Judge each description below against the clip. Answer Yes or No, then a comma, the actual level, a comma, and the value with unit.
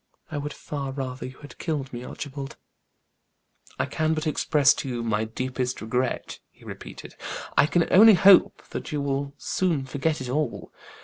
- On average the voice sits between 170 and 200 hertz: No, medium, 140 Hz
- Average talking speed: Yes, average, 165 wpm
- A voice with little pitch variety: No, average, 3.1 semitones